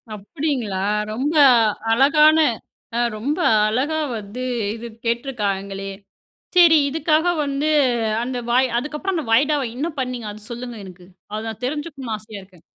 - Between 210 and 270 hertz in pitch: Yes, very high, 255 Hz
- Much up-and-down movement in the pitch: Yes, wide, 5.8 semitones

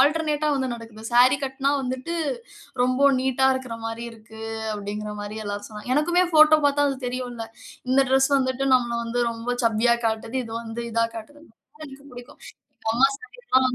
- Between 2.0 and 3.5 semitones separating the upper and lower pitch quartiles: Yes, average, 3.1 semitones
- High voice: Yes, very high, 255 Hz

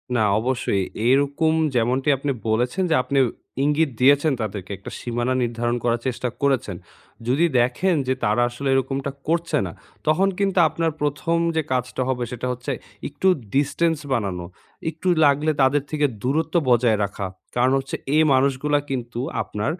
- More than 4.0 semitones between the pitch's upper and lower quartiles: No, average, 3.7 semitones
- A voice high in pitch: No, low, 130 Hz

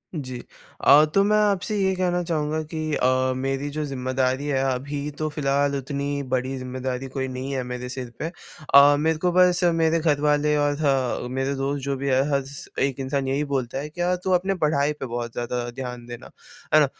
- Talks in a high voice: No, medium, 140 Hz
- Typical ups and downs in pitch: Yes, average, 3.0 semitones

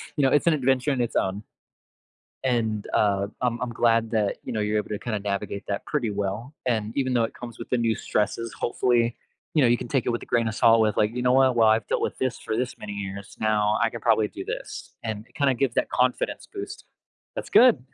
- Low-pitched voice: Yes, low, 115 Hz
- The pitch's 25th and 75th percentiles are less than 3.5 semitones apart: Yes, average, 2.9 semitones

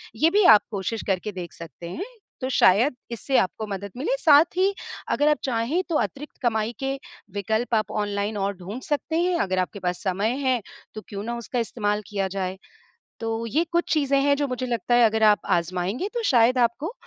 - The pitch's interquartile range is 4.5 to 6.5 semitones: Yes, wide, 5.5 semitones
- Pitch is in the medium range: No, high, 230 Hz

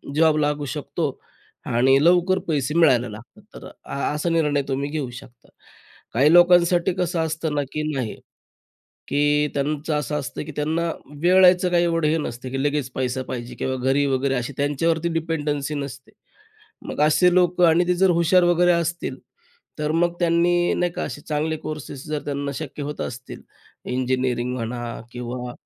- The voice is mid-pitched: Yes, medium, 150 Hz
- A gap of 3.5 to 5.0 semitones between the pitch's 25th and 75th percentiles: Yes, average, 4.2 semitones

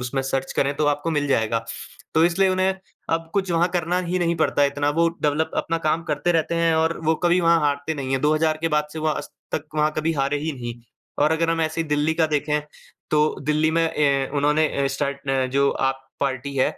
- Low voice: No, medium, 155 Hz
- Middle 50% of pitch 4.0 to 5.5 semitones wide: No, average, 2.7 semitones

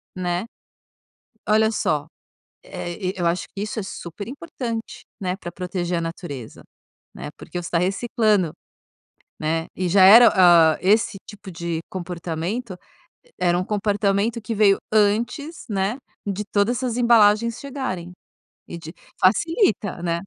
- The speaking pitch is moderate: No, high, 195 Hz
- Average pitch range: Yes, average, 4.1 semitones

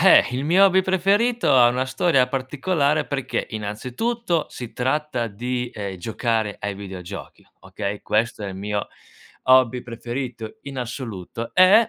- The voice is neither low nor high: No, low, 125 Hz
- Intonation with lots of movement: Yes, wide, 5.7 semitones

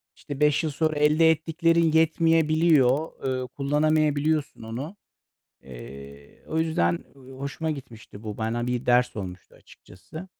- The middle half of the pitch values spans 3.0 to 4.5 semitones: No, average, 5.3 semitones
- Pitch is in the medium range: Yes, medium, 145 Hz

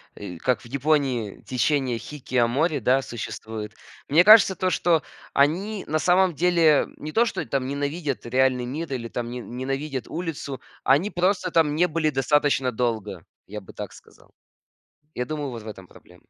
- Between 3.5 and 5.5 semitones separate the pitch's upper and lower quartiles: Yes, average, 4.7 semitones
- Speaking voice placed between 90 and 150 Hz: Yes, medium, 140 Hz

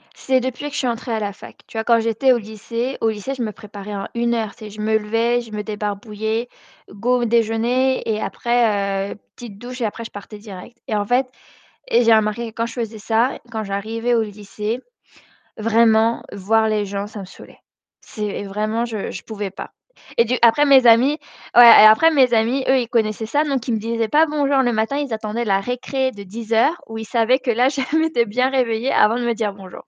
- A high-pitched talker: Yes, high, 225 Hz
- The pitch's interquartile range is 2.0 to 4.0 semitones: Yes, narrow, 2.4 semitones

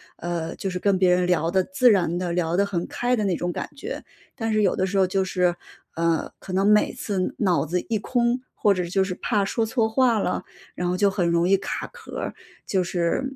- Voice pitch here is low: No, high, 190 Hz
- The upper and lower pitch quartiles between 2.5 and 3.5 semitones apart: Yes, average, 3.2 semitones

